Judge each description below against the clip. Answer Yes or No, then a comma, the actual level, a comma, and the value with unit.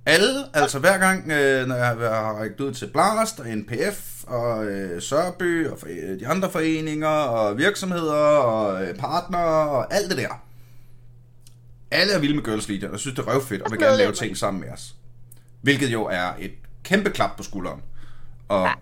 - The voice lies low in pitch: Yes, low, 125 Hz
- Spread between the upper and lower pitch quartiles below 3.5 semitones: No, average, 4.5 semitones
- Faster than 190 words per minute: No, average, 170 wpm